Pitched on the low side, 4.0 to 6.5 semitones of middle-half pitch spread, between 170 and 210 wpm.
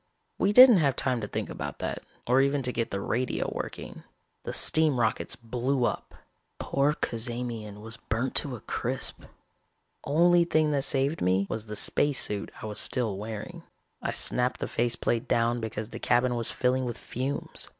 No: low, 125 Hz; average, 3.5 semitones; average, 175 wpm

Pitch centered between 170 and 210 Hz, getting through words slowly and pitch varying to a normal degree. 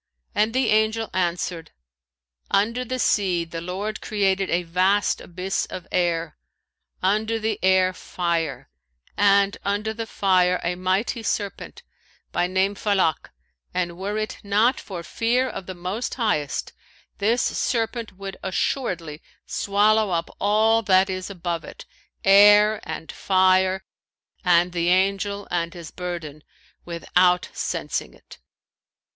Yes: high, 190 Hz; slow, 130 wpm; average, 3.0 semitones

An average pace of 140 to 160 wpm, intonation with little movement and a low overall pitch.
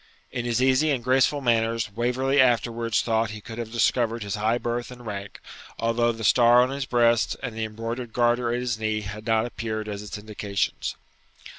No: average, 190 wpm; narrow, 1.8 semitones; low, 115 Hz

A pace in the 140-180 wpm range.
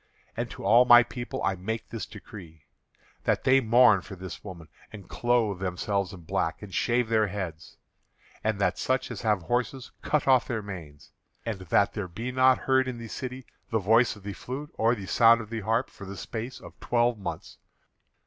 No: average, 195 wpm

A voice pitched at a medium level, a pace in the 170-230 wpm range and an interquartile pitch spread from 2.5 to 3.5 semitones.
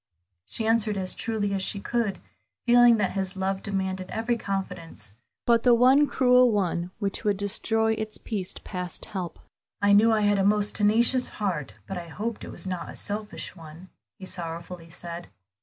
No: high, 205 Hz; average, 175 wpm; average, 3.1 semitones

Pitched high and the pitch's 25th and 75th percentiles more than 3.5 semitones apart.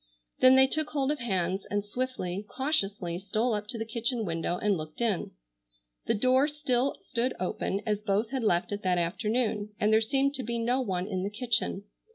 Yes: high, 220 Hz; average, 4.5 semitones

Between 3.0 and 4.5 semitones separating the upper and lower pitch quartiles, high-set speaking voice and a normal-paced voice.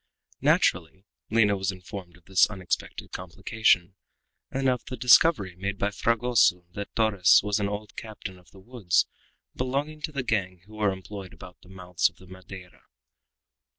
No: average, 3.5 semitones; low, 100 Hz; average, 160 wpm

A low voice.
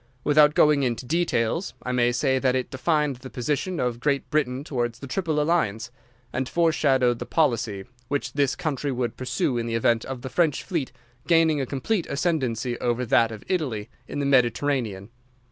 Yes: low, 130 Hz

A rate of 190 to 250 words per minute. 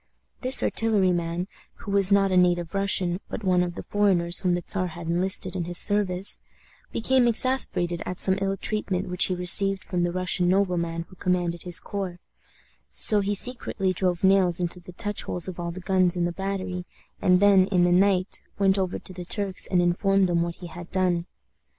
Yes: average, 195 wpm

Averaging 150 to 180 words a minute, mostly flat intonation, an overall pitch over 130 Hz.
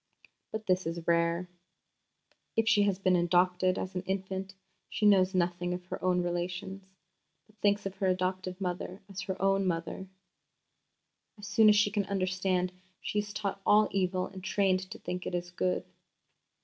Yes: average, 170 wpm; narrow, 1.6 semitones; medium, 185 Hz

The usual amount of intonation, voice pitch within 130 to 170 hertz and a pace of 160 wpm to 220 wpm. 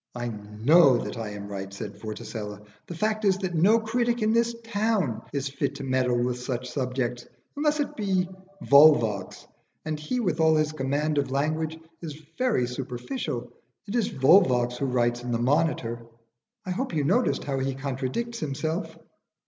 No: wide, 7.2 semitones; medium, 140 Hz; average, 170 wpm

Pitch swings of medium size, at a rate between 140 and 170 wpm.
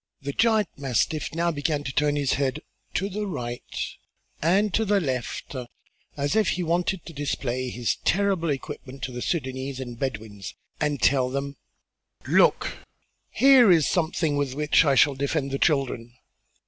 Yes: average, 4.5 semitones; average, 160 wpm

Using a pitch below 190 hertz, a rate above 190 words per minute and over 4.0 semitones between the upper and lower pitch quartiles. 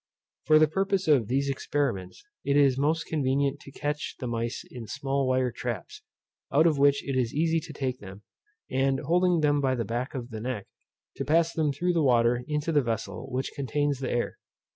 No: low, 135 Hz; average, 200 wpm; average, 3.2 semitones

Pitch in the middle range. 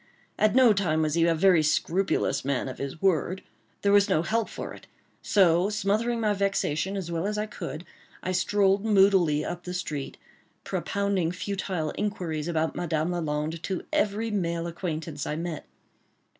Yes: medium, 180 Hz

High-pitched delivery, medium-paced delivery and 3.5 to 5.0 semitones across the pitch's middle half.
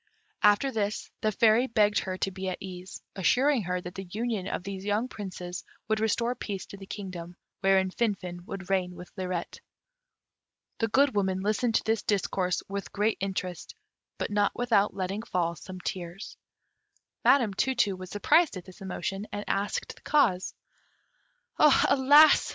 No: high, 200 Hz; average, 160 wpm; average, 3.0 semitones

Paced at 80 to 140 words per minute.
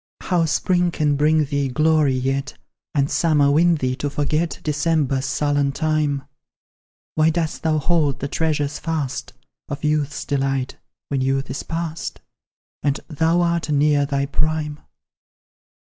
Yes: slow, 135 wpm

